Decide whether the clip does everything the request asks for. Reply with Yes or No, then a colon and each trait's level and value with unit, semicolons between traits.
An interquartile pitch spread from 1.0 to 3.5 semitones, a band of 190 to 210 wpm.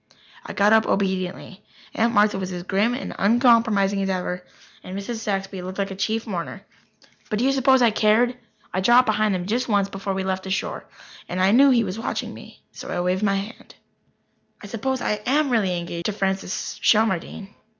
Yes: average, 3.0 semitones; average, 195 wpm